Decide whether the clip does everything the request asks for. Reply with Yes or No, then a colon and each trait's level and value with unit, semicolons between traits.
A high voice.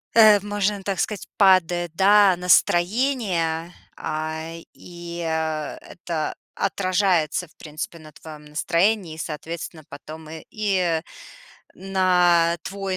No: medium, 175 Hz